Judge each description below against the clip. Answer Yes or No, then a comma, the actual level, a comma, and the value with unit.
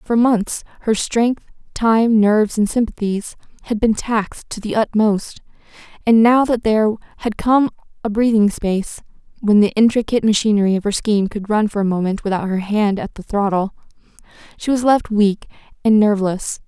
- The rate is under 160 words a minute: No, average, 170 wpm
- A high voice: Yes, high, 215 Hz